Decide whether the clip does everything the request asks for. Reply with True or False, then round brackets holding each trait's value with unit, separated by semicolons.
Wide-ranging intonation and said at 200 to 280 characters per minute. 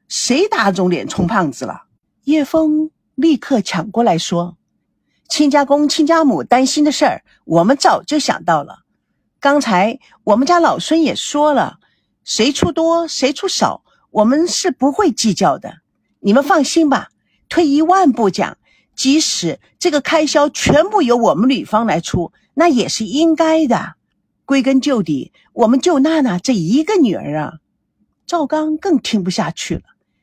True (6.4 semitones; 220 characters per minute)